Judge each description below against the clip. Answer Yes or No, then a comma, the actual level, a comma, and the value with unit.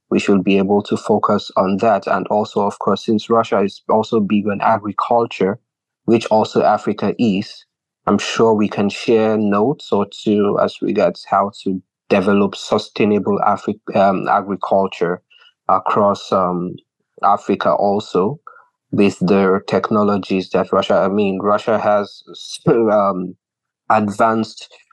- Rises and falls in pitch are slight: Yes, narrow, 1.9 semitones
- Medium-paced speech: No, slow, 130 wpm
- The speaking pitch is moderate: No, low, 105 Hz